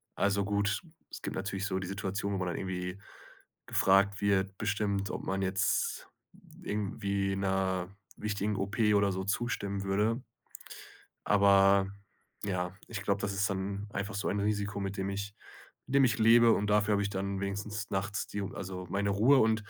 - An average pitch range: No, narrow, 1.0 semitones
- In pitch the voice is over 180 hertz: No, low, 100 Hz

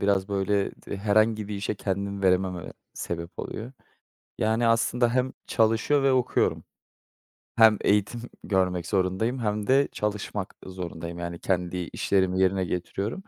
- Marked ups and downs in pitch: No, average, 3.3 semitones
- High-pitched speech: No, low, 100 Hz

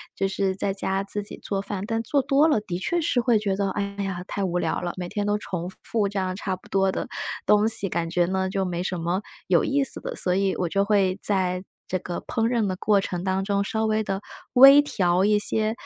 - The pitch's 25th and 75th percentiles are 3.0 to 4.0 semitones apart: No, narrow, 2.5 semitones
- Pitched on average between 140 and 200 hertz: Yes, high, 195 Hz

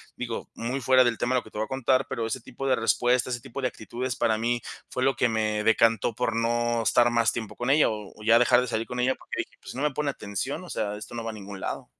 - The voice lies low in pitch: Yes, low, 120 Hz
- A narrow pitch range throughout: Yes, narrow, 2.3 semitones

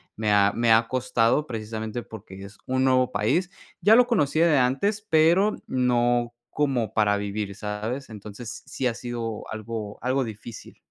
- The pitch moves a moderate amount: Yes, average, 3.7 semitones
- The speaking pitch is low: Yes, low, 120 Hz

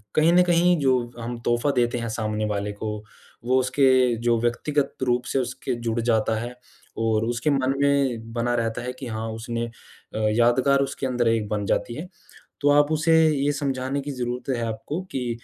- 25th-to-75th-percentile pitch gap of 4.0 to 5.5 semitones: No, average, 3.1 semitones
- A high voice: No, low, 120 Hz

